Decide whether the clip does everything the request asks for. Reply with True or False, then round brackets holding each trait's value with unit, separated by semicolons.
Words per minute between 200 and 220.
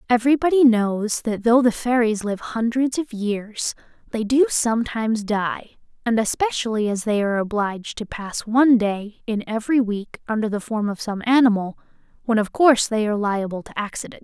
False (175 wpm)